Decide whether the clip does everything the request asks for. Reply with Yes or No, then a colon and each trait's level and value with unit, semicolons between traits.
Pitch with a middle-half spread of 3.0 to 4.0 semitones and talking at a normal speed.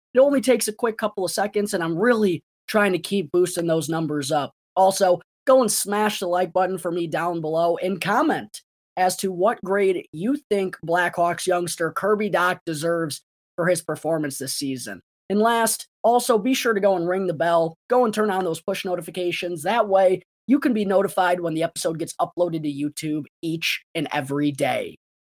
Yes: average, 3.6 semitones; average, 195 wpm